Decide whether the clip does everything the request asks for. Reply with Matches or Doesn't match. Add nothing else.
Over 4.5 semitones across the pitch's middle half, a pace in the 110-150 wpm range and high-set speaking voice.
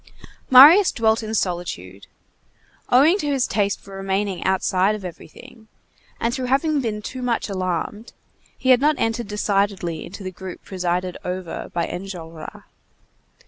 Matches